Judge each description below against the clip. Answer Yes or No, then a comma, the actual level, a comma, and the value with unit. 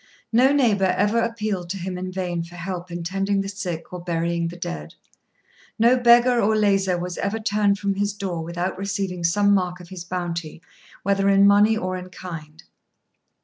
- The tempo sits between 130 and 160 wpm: No, average, 185 wpm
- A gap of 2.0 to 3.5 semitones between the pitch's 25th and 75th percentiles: Yes, average, 2.7 semitones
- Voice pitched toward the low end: No, high, 190 Hz